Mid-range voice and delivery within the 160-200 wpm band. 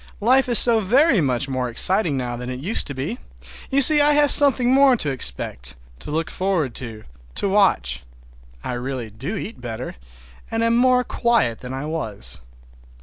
Yes: medium, 160 Hz; average, 175 wpm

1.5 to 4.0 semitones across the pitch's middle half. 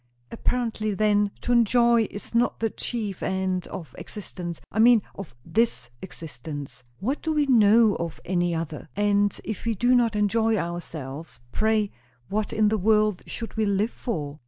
No: average, 4.4 semitones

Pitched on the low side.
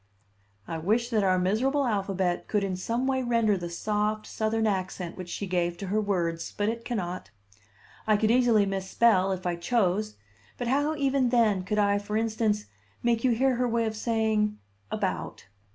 No: high, 215 Hz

